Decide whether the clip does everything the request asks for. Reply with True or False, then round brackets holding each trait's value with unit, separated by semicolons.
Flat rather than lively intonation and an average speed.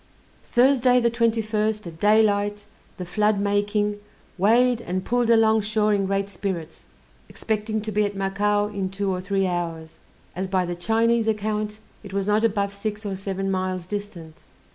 True (2.1 semitones; 165 wpm)